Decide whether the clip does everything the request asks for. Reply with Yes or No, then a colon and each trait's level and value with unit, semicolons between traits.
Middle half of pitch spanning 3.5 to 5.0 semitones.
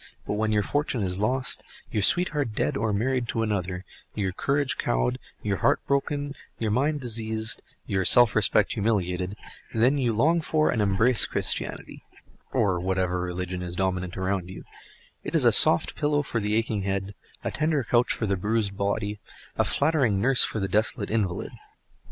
Yes: average, 4.6 semitones